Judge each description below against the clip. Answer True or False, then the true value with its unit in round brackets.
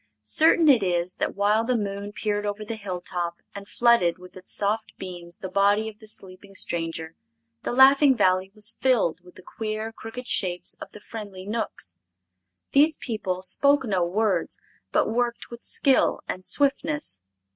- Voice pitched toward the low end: False (205 Hz)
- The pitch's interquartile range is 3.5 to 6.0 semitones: True (4.0 semitones)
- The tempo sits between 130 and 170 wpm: True (165 wpm)